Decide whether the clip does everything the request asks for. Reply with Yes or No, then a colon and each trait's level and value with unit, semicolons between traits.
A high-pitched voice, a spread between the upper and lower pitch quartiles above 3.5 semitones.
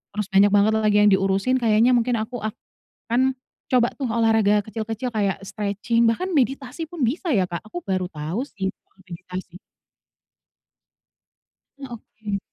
Yes: high, 215 Hz; average, 3.9 semitones